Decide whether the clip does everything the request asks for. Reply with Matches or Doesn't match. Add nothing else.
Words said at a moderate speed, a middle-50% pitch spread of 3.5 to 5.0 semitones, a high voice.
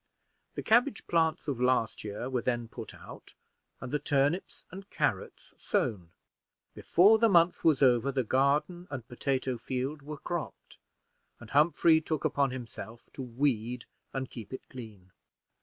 Doesn't match